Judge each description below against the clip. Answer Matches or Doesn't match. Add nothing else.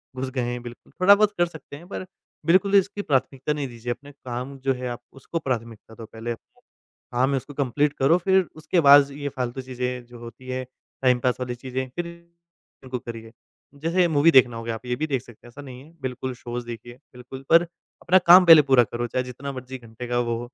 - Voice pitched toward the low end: Matches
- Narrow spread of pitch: Doesn't match